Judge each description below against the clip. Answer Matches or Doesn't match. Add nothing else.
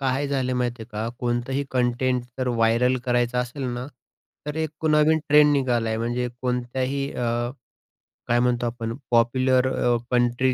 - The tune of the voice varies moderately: Doesn't match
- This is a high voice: Doesn't match